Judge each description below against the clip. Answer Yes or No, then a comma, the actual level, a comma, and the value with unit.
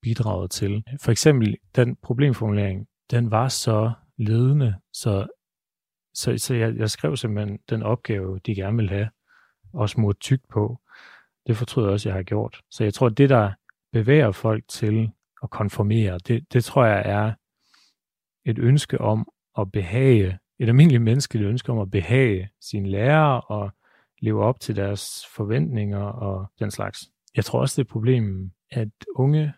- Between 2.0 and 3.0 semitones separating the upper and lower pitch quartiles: No, average, 3.4 semitones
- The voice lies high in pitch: No, low, 110 Hz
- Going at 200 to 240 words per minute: No, average, 165 wpm